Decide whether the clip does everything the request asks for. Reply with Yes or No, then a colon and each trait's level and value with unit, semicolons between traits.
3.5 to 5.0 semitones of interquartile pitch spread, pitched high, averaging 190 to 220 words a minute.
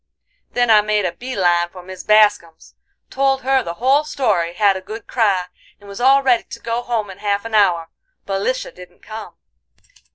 Yes: average, 4.5 semitones; high, 210 Hz; average, 195 wpm